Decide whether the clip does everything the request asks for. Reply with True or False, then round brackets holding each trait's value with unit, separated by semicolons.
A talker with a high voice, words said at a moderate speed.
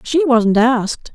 True (245 Hz; 155 wpm)